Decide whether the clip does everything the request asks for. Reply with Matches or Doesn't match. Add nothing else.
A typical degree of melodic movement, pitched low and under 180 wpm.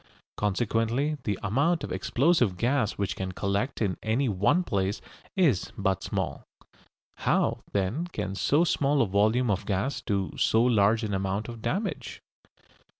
Doesn't match